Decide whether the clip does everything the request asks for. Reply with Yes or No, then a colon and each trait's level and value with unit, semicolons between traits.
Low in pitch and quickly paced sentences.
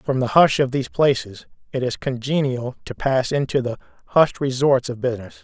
No: low, 130 Hz; average, 190 wpm